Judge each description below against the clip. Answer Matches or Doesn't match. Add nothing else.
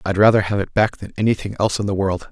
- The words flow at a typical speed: Doesn't match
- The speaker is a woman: Doesn't match